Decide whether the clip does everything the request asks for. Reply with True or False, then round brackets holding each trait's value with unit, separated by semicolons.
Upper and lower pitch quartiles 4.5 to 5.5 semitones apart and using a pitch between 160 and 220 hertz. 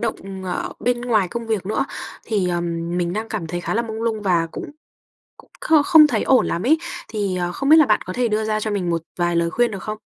True (4.8 semitones; 215 Hz)